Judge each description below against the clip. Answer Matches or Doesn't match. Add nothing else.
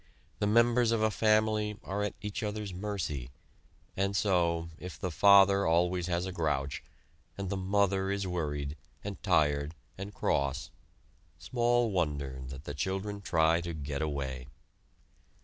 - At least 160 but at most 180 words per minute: Doesn't match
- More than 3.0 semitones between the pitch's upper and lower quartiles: Matches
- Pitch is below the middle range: Matches